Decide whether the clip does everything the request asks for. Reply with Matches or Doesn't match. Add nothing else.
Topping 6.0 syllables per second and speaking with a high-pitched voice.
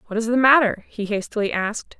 Matches